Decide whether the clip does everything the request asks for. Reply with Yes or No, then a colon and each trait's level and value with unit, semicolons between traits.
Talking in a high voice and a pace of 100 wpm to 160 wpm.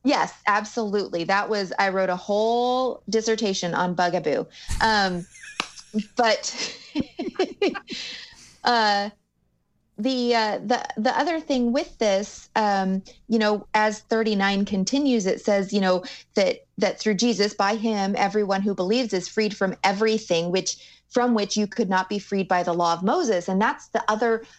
Yes: high, 215 Hz; average, 155 wpm